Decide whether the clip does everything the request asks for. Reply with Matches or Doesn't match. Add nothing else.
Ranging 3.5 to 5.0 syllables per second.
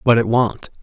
Matches